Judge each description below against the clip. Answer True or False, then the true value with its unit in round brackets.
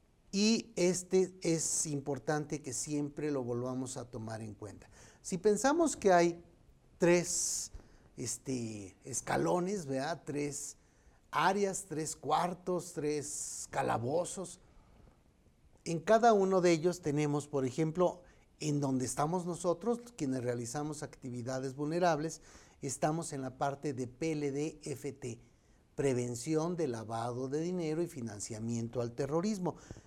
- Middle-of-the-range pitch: True (150 Hz)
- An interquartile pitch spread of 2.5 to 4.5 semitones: False (5.2 semitones)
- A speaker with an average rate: False (115 wpm)